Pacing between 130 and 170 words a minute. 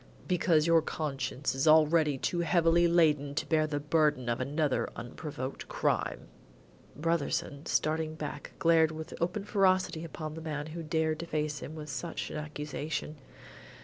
Yes: average, 150 wpm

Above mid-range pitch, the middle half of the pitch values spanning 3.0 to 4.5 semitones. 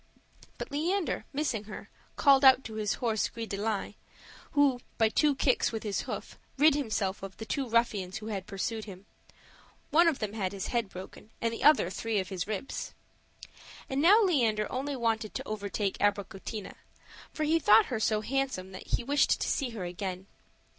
No: high, 220 Hz; average, 5.1 semitones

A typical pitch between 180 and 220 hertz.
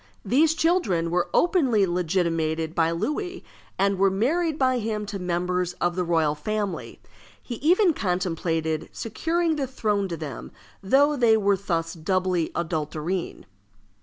Yes: high, 190 Hz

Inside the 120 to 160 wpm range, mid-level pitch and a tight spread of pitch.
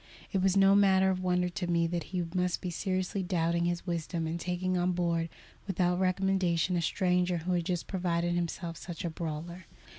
No: average, 190 wpm; medium, 180 Hz; narrow, 1.5 semitones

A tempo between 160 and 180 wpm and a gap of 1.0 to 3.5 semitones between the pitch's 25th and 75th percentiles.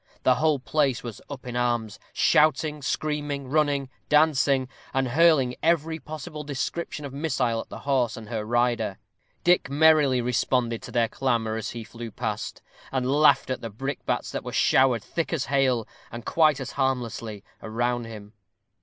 No: average, 165 wpm; average, 3.9 semitones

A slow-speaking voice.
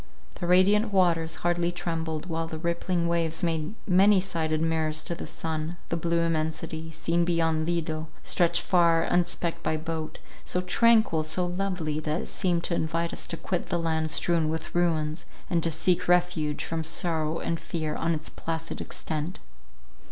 No: average, 165 wpm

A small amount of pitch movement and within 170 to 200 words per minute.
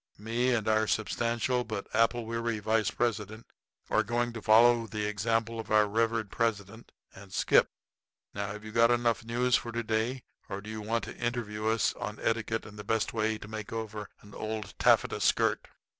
Yes: narrow, 1.6 semitones; average, 190 wpm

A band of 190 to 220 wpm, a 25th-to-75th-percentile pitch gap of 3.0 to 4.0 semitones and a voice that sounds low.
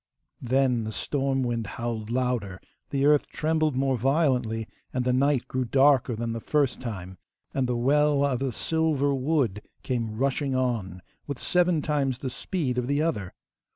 No: average, 165 wpm; average, 3.3 semitones; low, 130 Hz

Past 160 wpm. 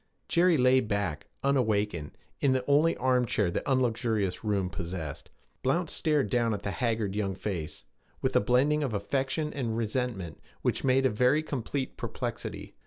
No: average, 155 wpm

